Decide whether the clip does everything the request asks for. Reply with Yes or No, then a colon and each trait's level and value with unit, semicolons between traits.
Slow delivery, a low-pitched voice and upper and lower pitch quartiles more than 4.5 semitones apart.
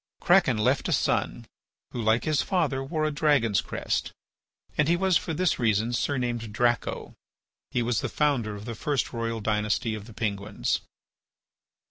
No: average, 160 wpm; low, 120 Hz; average, 5.3 semitones